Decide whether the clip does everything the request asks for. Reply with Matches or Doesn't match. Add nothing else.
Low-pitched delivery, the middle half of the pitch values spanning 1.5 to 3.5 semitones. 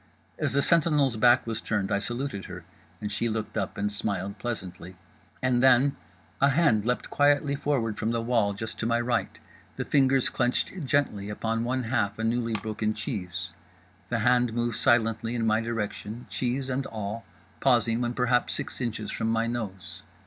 Matches